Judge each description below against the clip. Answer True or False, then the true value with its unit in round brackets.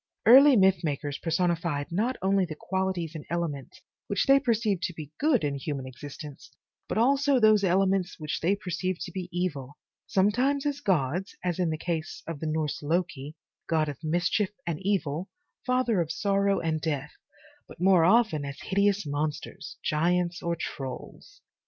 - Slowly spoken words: False (165 wpm)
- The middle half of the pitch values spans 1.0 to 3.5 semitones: False (4.4 semitones)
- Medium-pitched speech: True (175 Hz)